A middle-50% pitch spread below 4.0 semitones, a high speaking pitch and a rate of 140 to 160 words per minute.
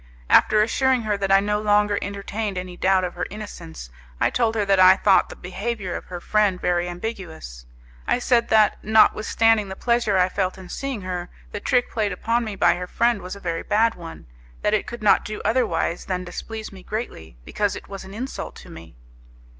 No: average, 3.3 semitones; high, 200 Hz; fast, 205 wpm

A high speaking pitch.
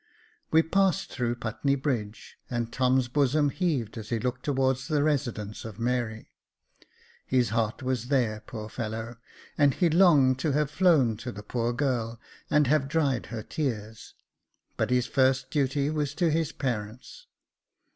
No: low, 130 Hz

